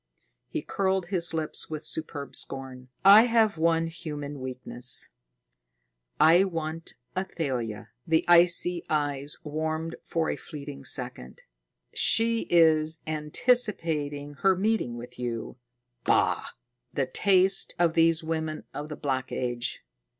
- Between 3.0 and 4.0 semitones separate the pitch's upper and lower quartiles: Yes, average, 3.6 semitones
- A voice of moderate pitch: Yes, medium, 160 Hz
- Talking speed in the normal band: No, slow, 120 wpm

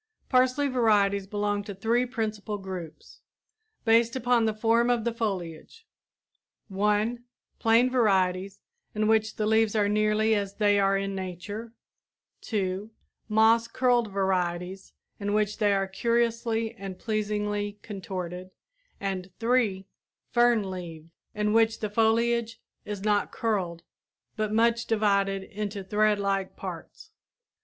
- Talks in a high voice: Yes, high, 210 Hz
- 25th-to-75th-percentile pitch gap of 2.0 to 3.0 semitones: Yes, narrow, 2.5 semitones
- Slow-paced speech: Yes, slow, 125 wpm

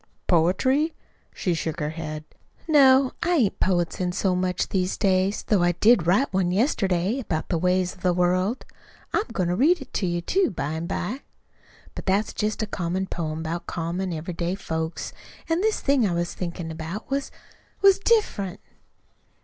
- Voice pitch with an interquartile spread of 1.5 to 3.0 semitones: No, average, 5.1 semitones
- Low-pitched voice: No, medium, 185 Hz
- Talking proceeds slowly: No, average, 175 wpm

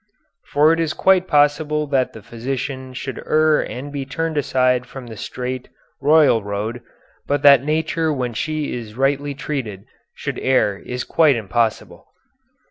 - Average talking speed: Yes, average, 150 wpm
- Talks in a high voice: No, low, 135 Hz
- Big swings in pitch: No, average, 3.6 semitones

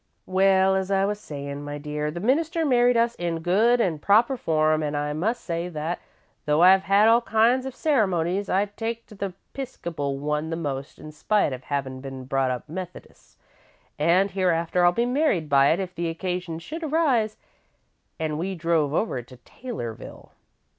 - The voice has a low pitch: No, medium, 180 Hz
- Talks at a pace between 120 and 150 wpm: No, average, 180 wpm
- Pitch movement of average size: No, wide, 6.3 semitones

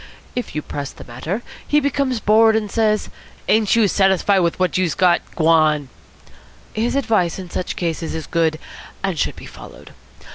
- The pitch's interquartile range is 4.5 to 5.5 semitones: Yes, average, 5.1 semitones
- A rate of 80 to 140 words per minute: No, average, 170 wpm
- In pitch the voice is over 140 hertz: Yes, high, 190 Hz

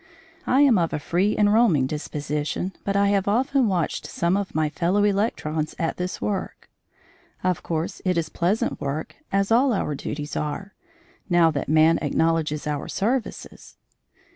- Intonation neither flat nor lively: Yes, average, 4.7 semitones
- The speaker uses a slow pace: No, average, 160 wpm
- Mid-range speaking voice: Yes, medium, 175 Hz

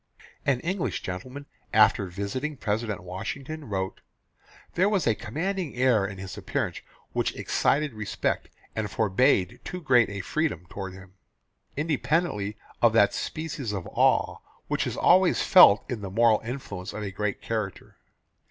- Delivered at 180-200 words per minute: No, average, 145 wpm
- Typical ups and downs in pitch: No, wide, 6.6 semitones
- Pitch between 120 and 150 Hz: No, low, 110 Hz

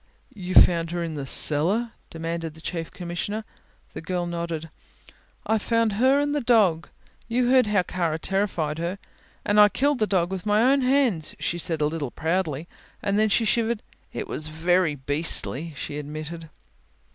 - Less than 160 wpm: No, average, 170 wpm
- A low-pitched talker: No, medium, 175 Hz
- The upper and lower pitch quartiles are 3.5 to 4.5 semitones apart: No, average, 5.0 semitones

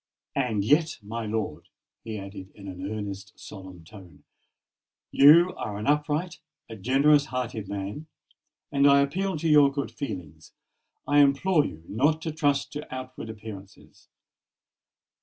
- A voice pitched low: Yes, low, 125 Hz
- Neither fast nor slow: No, slow, 130 wpm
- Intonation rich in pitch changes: Yes, wide, 6.6 semitones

